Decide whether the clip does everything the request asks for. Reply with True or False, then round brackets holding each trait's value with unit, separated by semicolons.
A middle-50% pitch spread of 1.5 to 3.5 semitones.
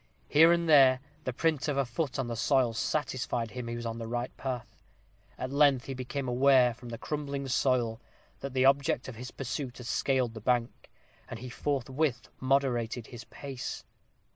True (2.5 semitones)